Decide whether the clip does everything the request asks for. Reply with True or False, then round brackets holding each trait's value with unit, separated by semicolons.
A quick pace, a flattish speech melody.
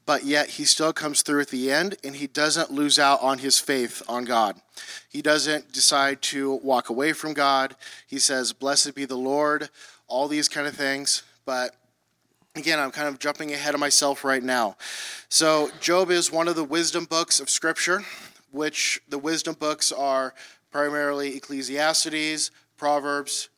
False (170 wpm; 2.0 semitones)